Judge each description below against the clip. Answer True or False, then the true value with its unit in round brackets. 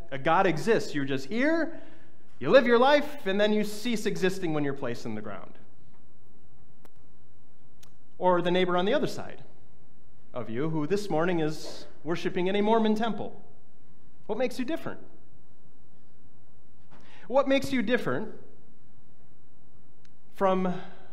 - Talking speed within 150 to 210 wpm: False (135 wpm)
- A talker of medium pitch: False (195 Hz)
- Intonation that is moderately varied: False (6.3 semitones)